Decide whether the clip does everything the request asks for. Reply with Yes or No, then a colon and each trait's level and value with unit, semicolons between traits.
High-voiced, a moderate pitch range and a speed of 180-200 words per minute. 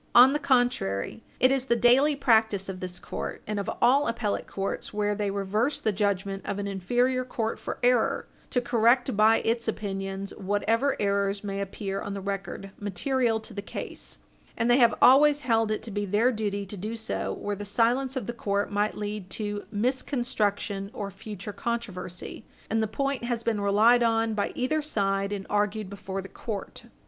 Yes: high, 210 Hz; average, 3.2 semitones; average, 185 wpm